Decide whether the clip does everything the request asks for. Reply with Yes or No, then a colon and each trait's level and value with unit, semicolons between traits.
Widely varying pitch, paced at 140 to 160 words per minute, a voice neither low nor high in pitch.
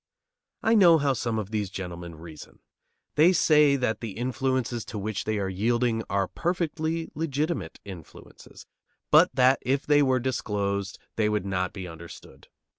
No: wide, 6.3 semitones; average, 155 wpm; low, 115 Hz